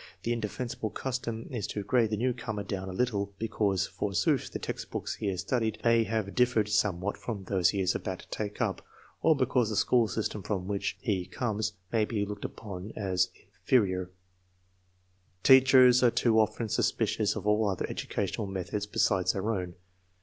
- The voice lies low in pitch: Yes, low, 105 Hz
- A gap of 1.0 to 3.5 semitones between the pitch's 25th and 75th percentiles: Yes, average, 3.0 semitones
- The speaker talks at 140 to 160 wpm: No, average, 170 wpm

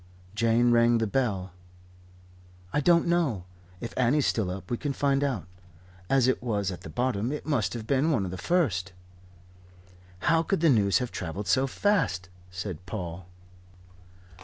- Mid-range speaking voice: No, low, 115 Hz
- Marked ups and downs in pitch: Yes, wide, 6.2 semitones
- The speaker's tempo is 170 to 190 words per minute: No, average, 160 wpm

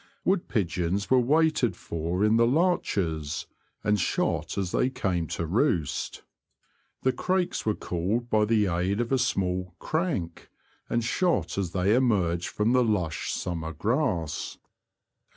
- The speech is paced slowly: No, average, 145 wpm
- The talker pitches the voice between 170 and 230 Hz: No, low, 105 Hz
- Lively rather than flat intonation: Yes, wide, 6.3 semitones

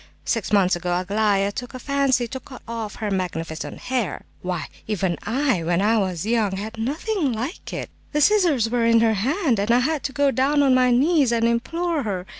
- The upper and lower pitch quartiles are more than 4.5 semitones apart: Yes, average, 5.2 semitones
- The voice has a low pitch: No, high, 230 Hz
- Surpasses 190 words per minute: Yes, fast, 205 wpm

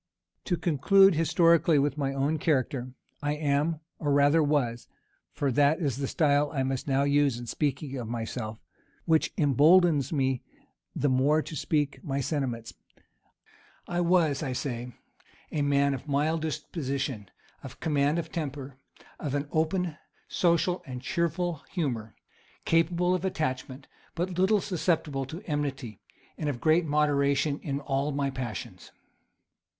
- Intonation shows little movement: No, average, 3.1 semitones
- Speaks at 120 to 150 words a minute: Yes, average, 140 wpm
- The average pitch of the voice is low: No, medium, 145 Hz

